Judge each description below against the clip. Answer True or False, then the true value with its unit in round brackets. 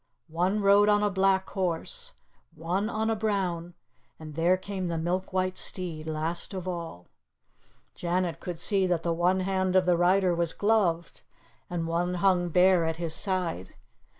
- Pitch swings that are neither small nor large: False (2.2 semitones)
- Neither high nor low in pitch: True (180 Hz)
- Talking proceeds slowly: False (160 wpm)